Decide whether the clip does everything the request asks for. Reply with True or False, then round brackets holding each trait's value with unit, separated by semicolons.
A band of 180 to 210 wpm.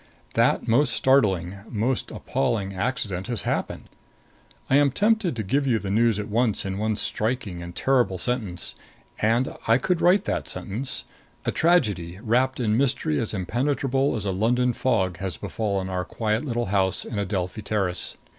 False (165 wpm)